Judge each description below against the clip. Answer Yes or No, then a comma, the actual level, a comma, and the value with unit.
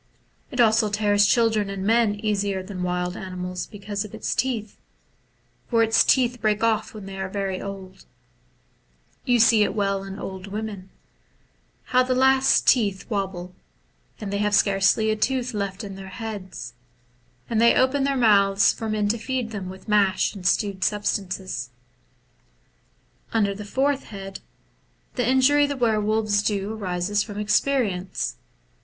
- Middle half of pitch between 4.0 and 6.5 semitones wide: No, average, 2.7 semitones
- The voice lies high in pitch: Yes, high, 205 Hz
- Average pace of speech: Yes, average, 155 wpm